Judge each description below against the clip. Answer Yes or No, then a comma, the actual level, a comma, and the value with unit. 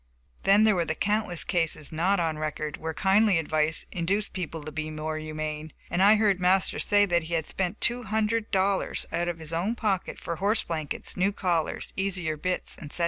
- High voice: No, medium, 175 Hz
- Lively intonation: No, average, 4.0 semitones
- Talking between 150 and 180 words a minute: No, average, 195 wpm